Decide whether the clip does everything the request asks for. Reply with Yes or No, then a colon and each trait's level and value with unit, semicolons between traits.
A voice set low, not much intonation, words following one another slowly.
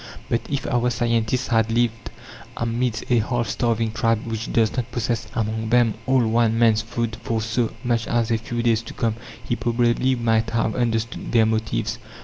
No: low, 115 Hz; narrow, 1.1 semitones; average, 180 wpm